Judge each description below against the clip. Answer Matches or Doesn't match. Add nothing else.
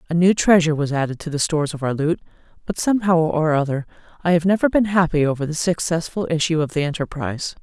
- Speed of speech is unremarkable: Doesn't match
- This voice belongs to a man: Doesn't match